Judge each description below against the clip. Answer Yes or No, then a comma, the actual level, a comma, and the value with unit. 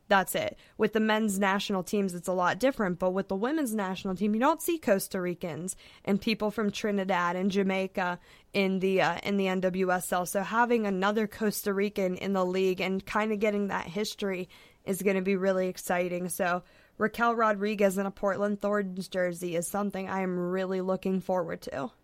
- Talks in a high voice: Yes, high, 195 Hz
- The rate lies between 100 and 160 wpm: No, average, 190 wpm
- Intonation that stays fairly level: Yes, narrow, 2.0 semitones